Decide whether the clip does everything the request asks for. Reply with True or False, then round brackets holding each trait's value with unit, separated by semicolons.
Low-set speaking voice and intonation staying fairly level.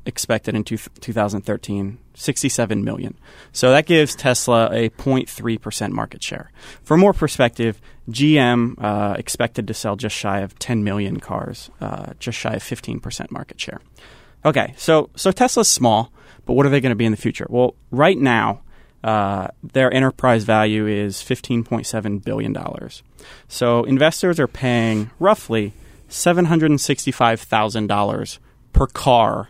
False (120 Hz; 3.8 semitones)